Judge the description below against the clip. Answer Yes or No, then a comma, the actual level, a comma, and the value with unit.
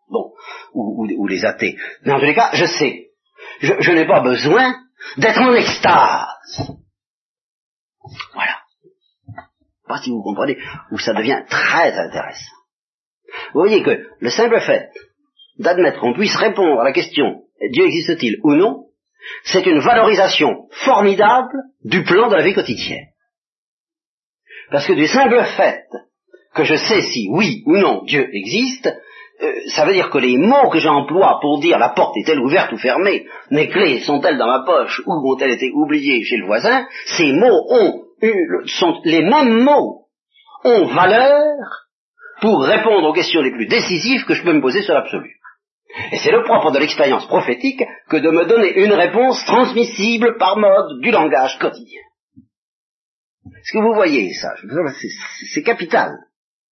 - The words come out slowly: No, average, 160 wpm